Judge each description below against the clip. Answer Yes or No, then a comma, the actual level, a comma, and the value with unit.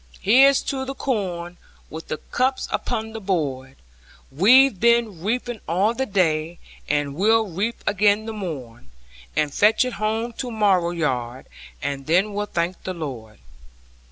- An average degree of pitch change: No, wide, 6.1 semitones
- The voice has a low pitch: No, high, 195 Hz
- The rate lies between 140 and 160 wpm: Yes, average, 150 wpm